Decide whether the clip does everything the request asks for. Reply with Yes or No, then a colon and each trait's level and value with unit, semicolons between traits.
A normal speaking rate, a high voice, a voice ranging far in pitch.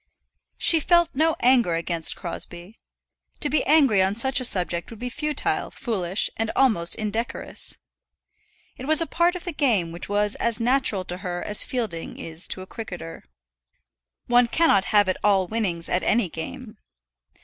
Yes: average, 165 wpm; high, 220 Hz; wide, 6.4 semitones